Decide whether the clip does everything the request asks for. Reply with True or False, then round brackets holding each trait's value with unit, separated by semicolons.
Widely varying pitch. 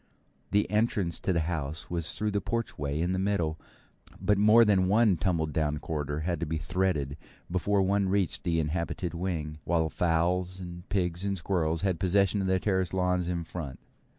False (3.0 semitones)